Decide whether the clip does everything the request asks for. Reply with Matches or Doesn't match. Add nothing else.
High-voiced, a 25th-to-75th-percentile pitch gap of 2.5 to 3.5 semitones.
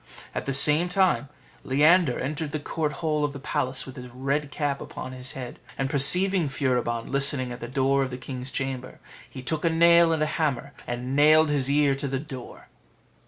Doesn't match